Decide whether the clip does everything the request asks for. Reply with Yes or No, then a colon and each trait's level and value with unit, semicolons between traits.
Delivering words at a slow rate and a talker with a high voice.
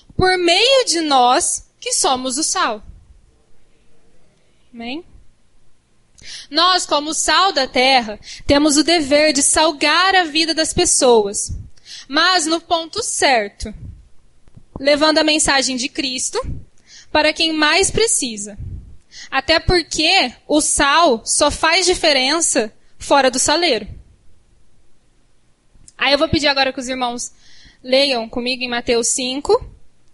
Yes: slow, 115 wpm; very high, 305 Hz